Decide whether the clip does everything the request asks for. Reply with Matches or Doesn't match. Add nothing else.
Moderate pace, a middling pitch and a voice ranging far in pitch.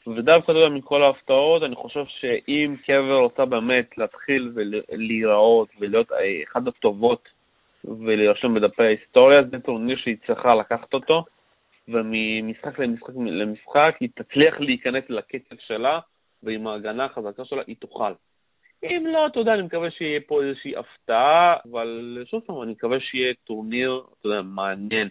Doesn't match